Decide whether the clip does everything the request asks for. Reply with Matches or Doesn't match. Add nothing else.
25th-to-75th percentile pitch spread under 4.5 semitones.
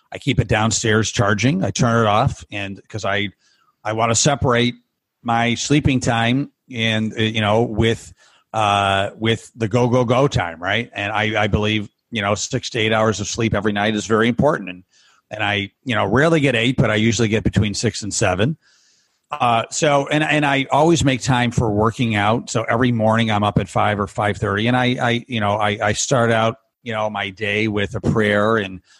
Matches